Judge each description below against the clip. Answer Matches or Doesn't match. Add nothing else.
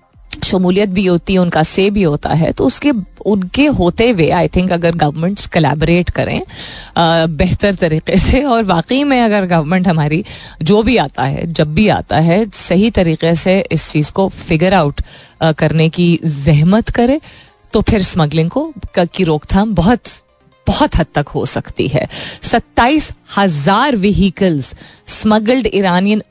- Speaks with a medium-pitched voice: Matches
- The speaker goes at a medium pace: Matches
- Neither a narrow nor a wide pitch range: Matches